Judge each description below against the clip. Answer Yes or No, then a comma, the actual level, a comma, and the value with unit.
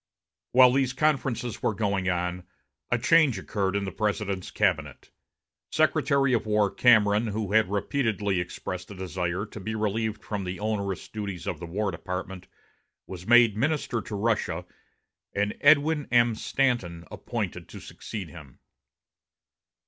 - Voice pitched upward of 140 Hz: No, low, 105 Hz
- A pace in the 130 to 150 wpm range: Yes, average, 140 wpm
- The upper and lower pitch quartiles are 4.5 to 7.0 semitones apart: No, average, 4.0 semitones